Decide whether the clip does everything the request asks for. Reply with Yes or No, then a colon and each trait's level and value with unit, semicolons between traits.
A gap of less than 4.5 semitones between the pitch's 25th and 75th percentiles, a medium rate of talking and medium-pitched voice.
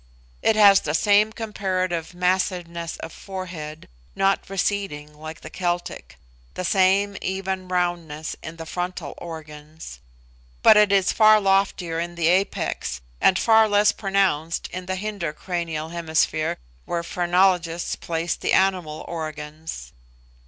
No: average, 3.2 semitones; slow, 130 wpm; medium, 175 Hz